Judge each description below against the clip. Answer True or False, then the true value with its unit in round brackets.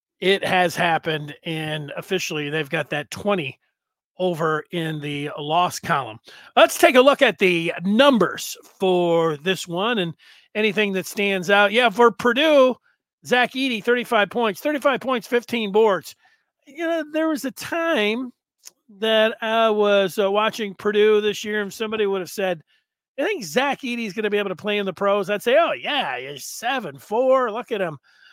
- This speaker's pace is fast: False (175 wpm)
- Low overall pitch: False (210 Hz)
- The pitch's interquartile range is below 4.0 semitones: False (5.1 semitones)